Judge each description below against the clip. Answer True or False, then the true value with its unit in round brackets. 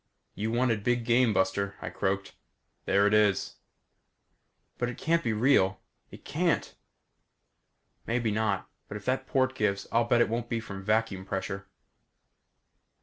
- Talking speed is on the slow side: False (145 wpm)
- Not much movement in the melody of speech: False (3.3 semitones)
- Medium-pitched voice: False (110 Hz)